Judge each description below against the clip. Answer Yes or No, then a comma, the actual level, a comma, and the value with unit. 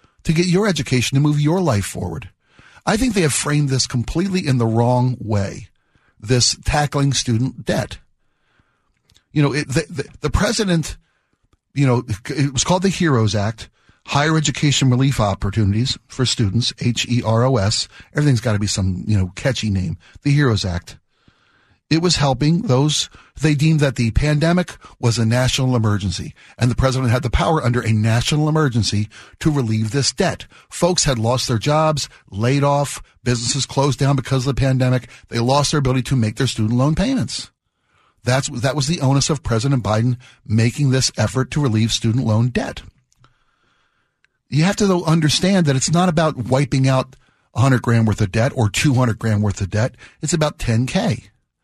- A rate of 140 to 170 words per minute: No, average, 180 wpm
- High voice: No, low, 130 Hz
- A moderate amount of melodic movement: Yes, average, 4.6 semitones